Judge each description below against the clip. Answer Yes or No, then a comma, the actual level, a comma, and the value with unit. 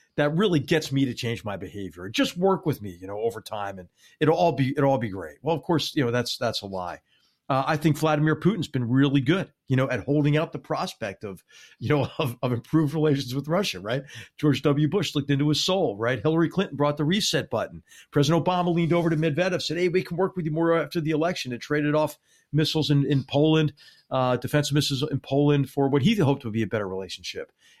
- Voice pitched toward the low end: No, medium, 150 Hz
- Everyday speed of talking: No, fast, 235 wpm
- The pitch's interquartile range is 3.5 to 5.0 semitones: Yes, average, 4.0 semitones